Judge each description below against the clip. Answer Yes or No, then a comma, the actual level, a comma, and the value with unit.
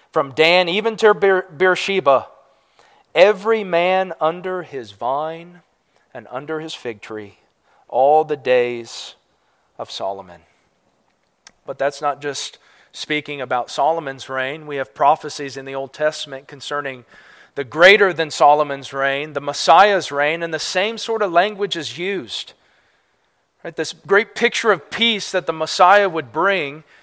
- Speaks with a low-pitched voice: No, medium, 155 Hz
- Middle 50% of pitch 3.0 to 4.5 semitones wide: No, average, 5.2 semitones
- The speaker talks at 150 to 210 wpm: No, average, 140 wpm